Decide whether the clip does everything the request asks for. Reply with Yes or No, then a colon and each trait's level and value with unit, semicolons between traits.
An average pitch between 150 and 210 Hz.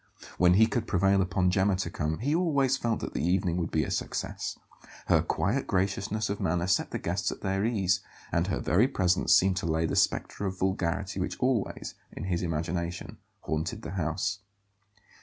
No: very low, 95 Hz